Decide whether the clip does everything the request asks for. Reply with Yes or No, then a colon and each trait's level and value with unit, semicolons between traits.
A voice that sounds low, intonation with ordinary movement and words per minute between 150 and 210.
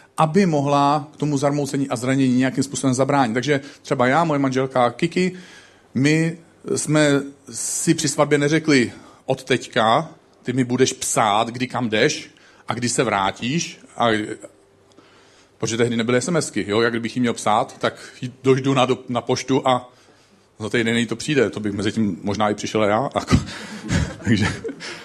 Yes: low, 130 Hz; average, 3.4 semitones; average, 160 wpm